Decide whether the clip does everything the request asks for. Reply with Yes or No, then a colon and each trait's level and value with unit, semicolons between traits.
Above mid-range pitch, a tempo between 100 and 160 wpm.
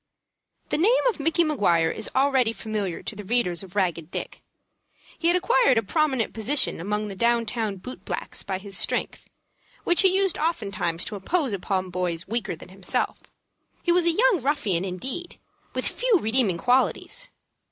No: high, 225 Hz; average, 170 wpm